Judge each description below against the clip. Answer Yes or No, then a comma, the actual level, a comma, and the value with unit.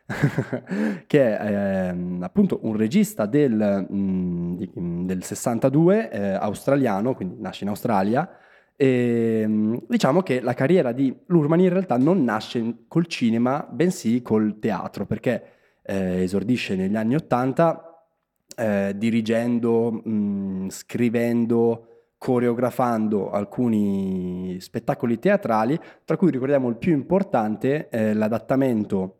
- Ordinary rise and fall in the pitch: No, wide, 5.9 semitones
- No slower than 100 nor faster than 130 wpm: Yes, slow, 115 wpm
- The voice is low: Yes, low, 115 Hz